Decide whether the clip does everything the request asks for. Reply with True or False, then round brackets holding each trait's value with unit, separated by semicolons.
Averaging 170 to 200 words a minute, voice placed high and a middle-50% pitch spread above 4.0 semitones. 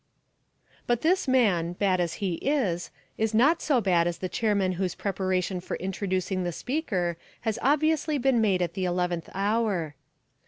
False (160 wpm; 195 Hz; 5.1 semitones)